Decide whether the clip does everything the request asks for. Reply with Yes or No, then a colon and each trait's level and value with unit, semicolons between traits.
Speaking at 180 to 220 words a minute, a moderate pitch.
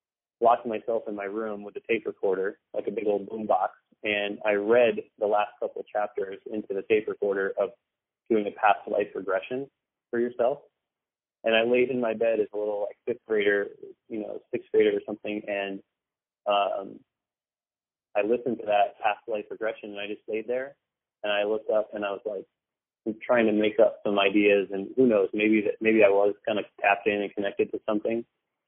No: average, 200 wpm; low, 110 Hz